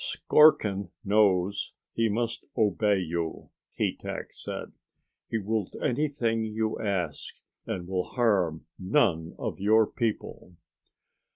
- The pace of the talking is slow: Yes, slow, 110 wpm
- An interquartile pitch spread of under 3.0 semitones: No, average, 3.5 semitones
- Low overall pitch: Yes, low, 105 Hz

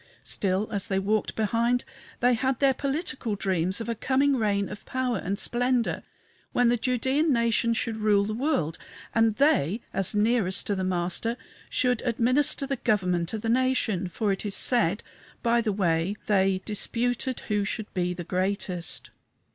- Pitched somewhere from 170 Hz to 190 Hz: No, high, 220 Hz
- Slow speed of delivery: No, average, 165 wpm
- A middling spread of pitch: Yes, average, 4.2 semitones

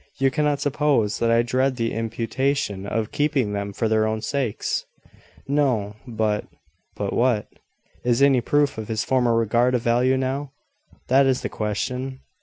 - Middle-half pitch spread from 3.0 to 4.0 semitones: Yes, average, 3.4 semitones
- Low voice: Yes, low, 120 Hz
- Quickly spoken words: No, average, 165 wpm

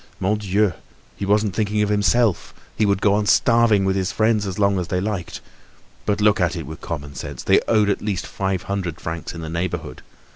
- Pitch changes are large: No, narrow, 2.5 semitones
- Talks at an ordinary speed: No, fast, 215 wpm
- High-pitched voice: No, low, 100 Hz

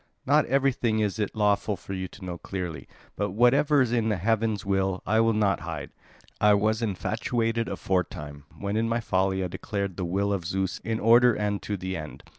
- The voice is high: No, low, 105 Hz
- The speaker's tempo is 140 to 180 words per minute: No, average, 190 wpm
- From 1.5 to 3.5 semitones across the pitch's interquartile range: Yes, average, 3.2 semitones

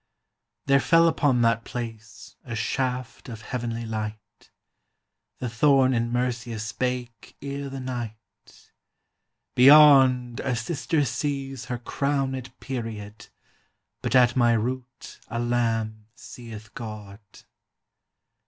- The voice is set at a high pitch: No, low, 120 Hz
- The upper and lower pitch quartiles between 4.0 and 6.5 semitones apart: No, average, 2.7 semitones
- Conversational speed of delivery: No, slow, 105 wpm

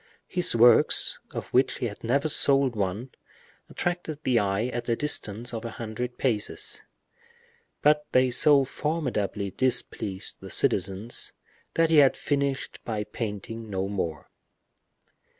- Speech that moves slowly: Yes, slow, 130 wpm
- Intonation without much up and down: No, average, 4.9 semitones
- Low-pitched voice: Yes, low, 120 Hz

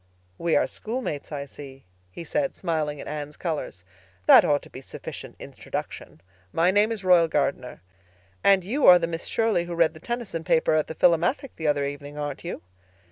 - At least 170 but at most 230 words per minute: Yes, average, 190 wpm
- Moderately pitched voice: Yes, medium, 165 Hz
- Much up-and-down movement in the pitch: No, average, 3.9 semitones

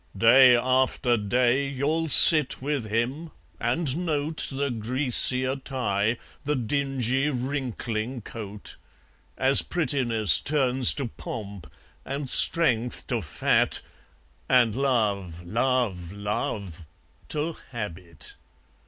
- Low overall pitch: Yes, low, 125 Hz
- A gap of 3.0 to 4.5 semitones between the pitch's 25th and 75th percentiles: Yes, average, 4.2 semitones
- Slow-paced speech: Yes, slow, 100 wpm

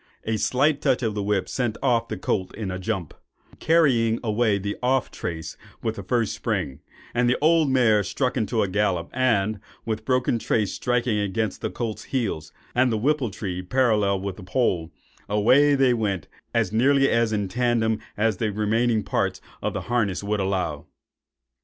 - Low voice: Yes, low, 110 Hz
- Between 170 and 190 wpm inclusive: Yes, average, 175 wpm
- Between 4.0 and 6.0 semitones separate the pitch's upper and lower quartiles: No, average, 3.5 semitones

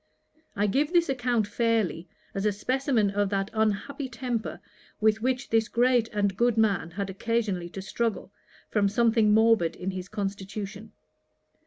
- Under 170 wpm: Yes, average, 150 wpm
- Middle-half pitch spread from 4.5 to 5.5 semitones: No, average, 3.0 semitones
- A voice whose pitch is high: Yes, high, 215 Hz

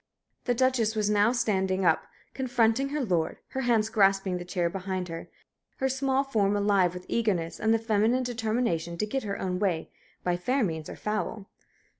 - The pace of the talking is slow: No, average, 180 wpm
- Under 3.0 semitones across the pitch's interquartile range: No, average, 4.7 semitones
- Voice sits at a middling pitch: No, high, 210 Hz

